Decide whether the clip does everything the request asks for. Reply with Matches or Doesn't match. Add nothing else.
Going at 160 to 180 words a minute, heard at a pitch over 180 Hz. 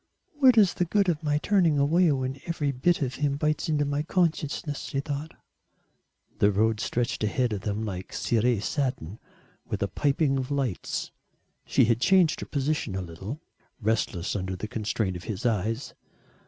Doesn't match